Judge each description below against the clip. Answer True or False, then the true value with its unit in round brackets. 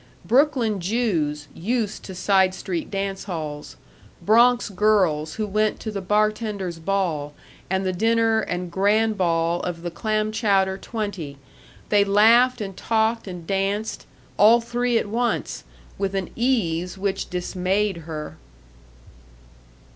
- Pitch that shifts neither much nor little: True (3.6 semitones)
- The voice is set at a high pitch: True (200 Hz)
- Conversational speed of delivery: False (125 wpm)